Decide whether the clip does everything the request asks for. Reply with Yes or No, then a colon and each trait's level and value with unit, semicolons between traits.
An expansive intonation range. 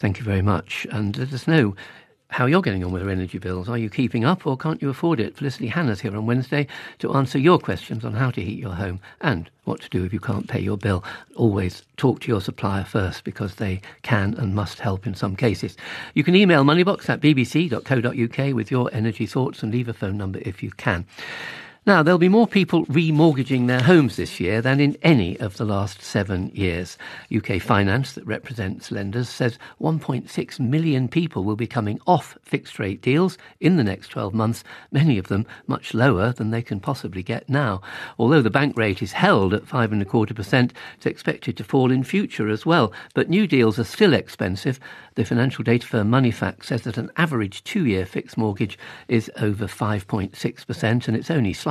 No: average, 4.6 semitones